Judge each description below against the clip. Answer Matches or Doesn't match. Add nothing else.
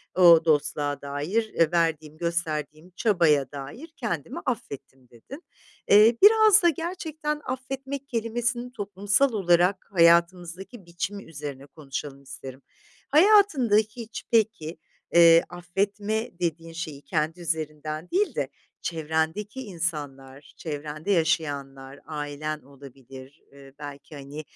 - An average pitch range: Doesn't match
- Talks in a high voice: Doesn't match